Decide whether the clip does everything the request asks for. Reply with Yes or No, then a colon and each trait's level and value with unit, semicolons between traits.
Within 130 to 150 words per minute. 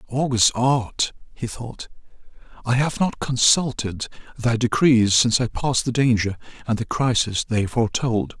Yes: average, 145 wpm